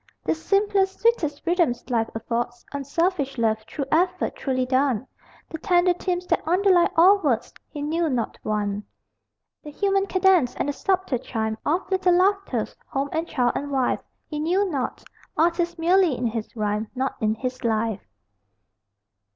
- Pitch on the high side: Yes, very high, 300 Hz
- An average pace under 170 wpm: Yes, average, 155 wpm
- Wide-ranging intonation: Yes, wide, 6.9 semitones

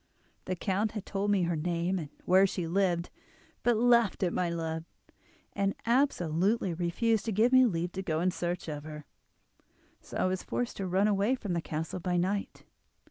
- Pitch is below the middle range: No, medium, 185 Hz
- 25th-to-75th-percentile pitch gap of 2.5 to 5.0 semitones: Yes, average, 3.3 semitones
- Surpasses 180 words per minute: Yes, average, 190 wpm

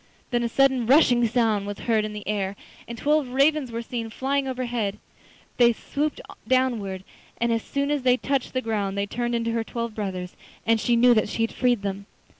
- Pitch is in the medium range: No, high, 235 Hz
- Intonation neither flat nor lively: Yes, average, 3.1 semitones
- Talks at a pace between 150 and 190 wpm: No, fast, 205 wpm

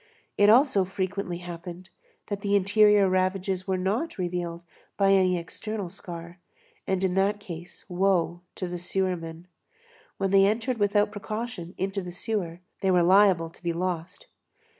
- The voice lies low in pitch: No, high, 190 Hz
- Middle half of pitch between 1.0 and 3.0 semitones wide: Yes, narrow, 2.4 semitones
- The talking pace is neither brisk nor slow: Yes, average, 150 wpm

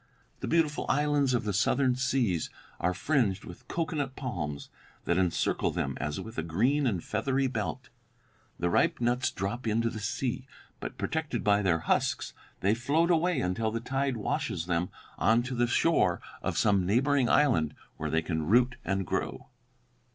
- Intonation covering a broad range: Yes, wide, 6.2 semitones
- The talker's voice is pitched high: No, low, 120 Hz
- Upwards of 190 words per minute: No, average, 170 wpm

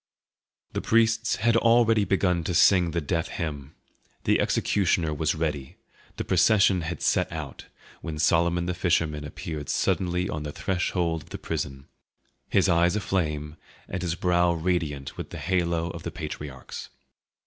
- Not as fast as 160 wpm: Yes, average, 150 wpm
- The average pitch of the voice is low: Yes, very low, 85 Hz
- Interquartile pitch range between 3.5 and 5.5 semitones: No, average, 3.1 semitones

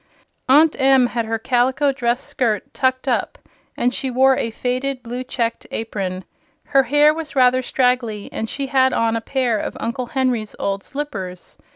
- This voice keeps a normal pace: Yes, average, 170 wpm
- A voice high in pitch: Yes, very high, 250 Hz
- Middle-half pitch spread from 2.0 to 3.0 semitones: Yes, average, 2.7 semitones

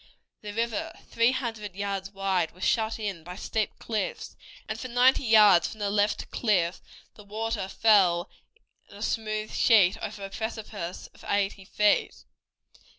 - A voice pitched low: No, high, 210 Hz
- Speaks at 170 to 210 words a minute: No, average, 150 wpm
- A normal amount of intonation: No, narrow, 2.3 semitones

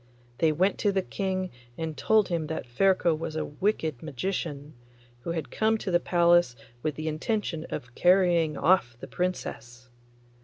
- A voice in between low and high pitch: Yes, medium, 170 Hz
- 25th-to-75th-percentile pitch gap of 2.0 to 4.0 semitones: Yes, average, 3.6 semitones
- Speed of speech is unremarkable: Yes, average, 160 wpm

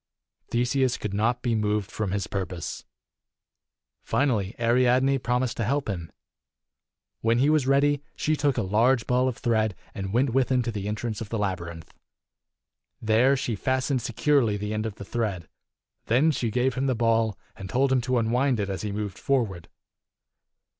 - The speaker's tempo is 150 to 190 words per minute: Yes, average, 175 wpm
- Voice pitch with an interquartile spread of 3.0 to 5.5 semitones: Yes, average, 3.8 semitones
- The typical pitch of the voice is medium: No, low, 115 Hz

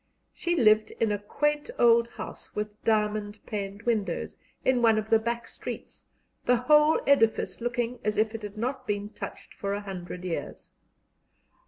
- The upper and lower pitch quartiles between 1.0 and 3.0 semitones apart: Yes, average, 2.7 semitones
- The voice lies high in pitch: Yes, high, 220 Hz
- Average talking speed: Yes, average, 165 wpm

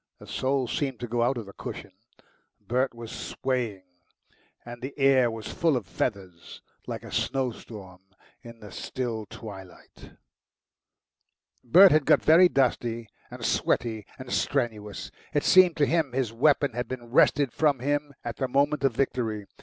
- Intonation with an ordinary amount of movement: Yes, average, 3.6 semitones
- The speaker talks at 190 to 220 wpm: No, average, 155 wpm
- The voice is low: Yes, low, 125 Hz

